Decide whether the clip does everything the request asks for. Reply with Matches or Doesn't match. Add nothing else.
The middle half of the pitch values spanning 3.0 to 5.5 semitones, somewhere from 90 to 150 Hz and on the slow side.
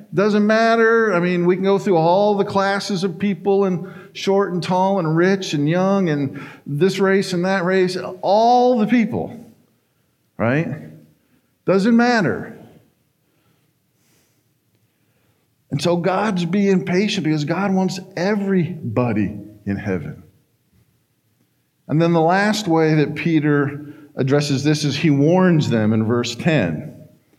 Doesn't match